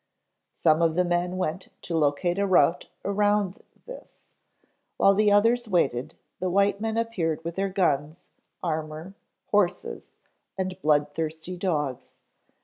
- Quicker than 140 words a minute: No, slow, 135 wpm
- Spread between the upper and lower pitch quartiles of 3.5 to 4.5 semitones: Yes, average, 4.0 semitones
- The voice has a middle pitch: Yes, medium, 180 Hz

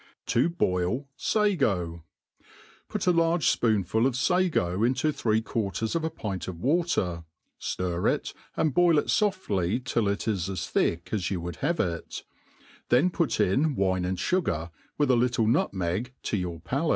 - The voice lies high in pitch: No, low, 115 Hz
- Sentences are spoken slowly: No, average, 165 wpm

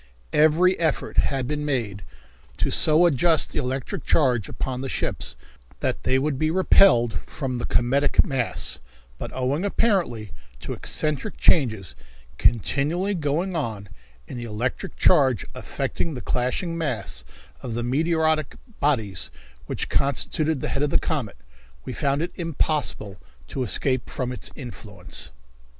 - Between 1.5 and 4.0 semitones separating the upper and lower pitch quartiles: No, average, 4.6 semitones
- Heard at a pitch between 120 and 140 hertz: Yes, low, 135 Hz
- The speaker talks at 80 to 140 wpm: Yes, slow, 135 wpm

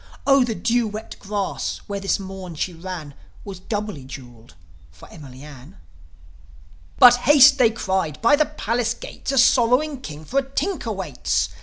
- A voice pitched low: No, high, 205 Hz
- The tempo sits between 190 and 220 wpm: No, average, 160 wpm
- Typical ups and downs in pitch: No, wide, 7.4 semitones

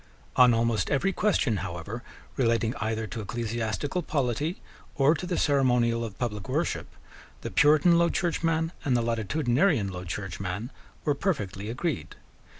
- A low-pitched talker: Yes, low, 120 Hz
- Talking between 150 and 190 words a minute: No, average, 140 wpm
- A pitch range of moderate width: No, wide, 5.7 semitones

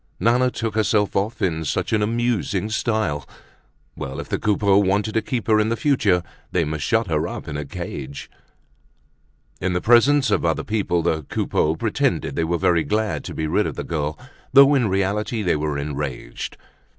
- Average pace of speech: Yes, average, 185 wpm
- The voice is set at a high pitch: No, low, 100 Hz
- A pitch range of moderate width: No, wide, 5.8 semitones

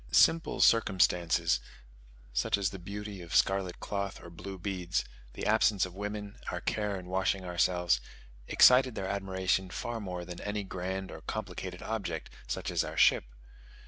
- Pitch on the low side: Yes, very low, 95 Hz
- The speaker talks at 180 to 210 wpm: No, average, 155 wpm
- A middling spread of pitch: No, narrow, 2.3 semitones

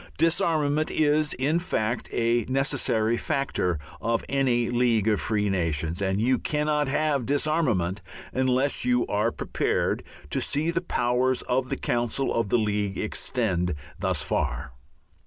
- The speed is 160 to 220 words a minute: No, average, 140 wpm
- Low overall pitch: Yes, low, 125 Hz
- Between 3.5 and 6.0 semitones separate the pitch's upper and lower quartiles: Yes, average, 5.0 semitones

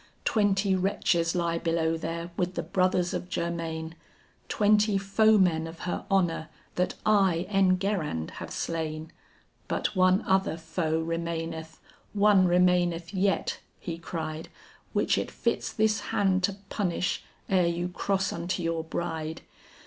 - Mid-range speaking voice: Yes, medium, 175 Hz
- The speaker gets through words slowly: Yes, slow, 130 wpm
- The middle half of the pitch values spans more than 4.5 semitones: No, average, 2.7 semitones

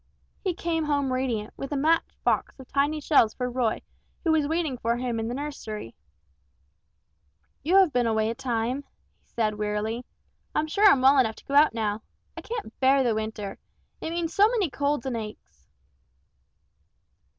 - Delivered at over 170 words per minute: Yes, average, 180 wpm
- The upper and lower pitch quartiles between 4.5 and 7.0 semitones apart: Yes, average, 5.2 semitones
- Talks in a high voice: Yes, very high, 260 Hz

